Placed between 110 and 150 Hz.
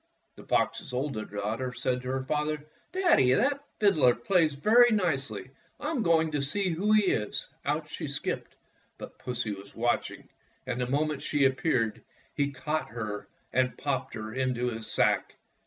Yes: low, 135 Hz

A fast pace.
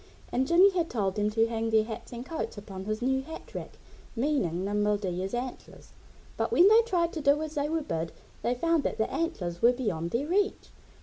Yes: fast, 210 wpm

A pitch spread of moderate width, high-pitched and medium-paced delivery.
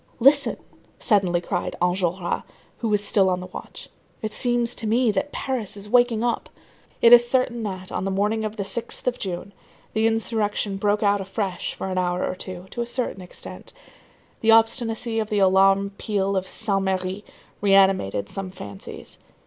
Yes: average, 3.0 semitones; high, 205 Hz; average, 175 wpm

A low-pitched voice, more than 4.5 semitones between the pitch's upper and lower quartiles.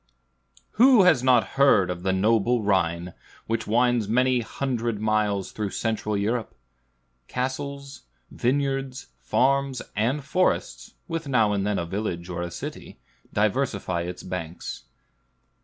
Yes: low, 110 Hz; average, 5.2 semitones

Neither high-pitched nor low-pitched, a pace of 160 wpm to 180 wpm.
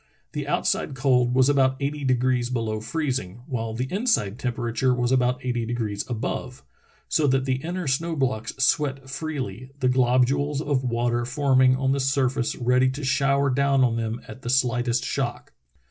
No: low, 130 Hz; average, 170 wpm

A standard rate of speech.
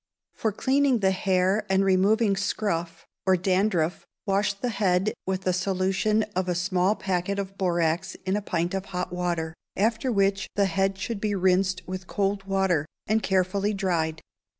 Yes: average, 165 wpm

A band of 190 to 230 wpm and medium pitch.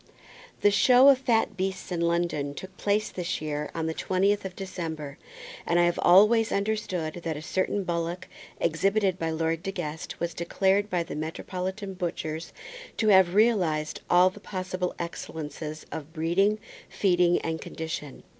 No: average, 160 wpm; medium, 175 Hz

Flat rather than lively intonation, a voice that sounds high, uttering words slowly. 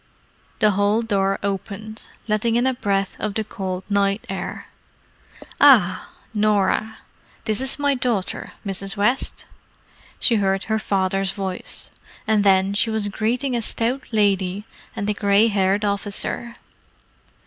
Yes: narrow, 2.1 semitones; high, 205 Hz; slow, 130 wpm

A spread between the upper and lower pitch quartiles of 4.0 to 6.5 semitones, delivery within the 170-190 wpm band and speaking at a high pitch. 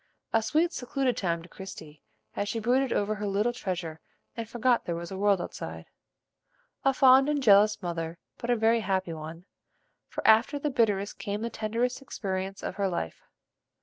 Yes: average, 4.4 semitones; average, 180 wpm; high, 210 Hz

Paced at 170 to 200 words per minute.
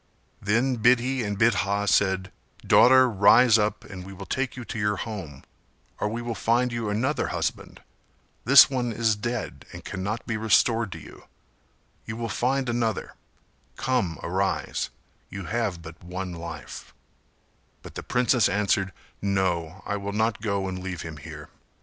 No: average, 155 wpm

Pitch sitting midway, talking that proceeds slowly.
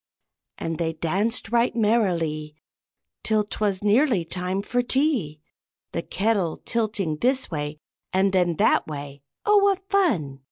No: high, 195 Hz; slow, 130 wpm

